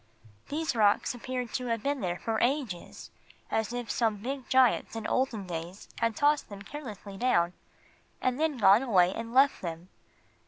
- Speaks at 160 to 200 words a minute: Yes, average, 165 wpm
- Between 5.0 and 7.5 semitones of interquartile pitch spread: No, average, 4.5 semitones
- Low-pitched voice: No, high, 230 Hz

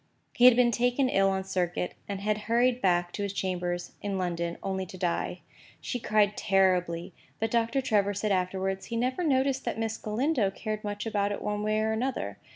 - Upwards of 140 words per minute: Yes, average, 195 wpm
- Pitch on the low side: No, high, 205 Hz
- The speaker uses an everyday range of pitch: Yes, average, 3.5 semitones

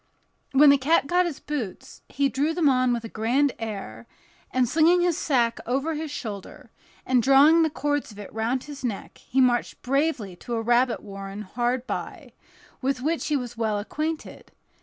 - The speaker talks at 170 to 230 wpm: Yes, average, 180 wpm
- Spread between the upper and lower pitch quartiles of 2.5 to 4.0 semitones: No, average, 4.4 semitones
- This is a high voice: Yes, very high, 255 Hz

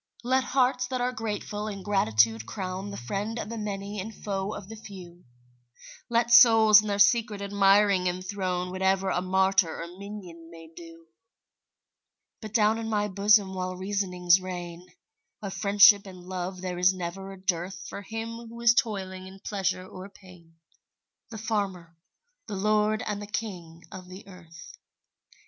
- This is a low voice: No, high, 195 Hz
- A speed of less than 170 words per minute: Yes, average, 160 wpm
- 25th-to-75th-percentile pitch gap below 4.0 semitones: Yes, narrow, 2.6 semitones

